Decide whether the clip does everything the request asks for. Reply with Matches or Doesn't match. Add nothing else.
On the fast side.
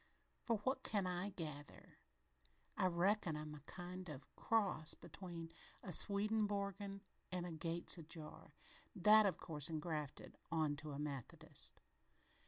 Doesn't match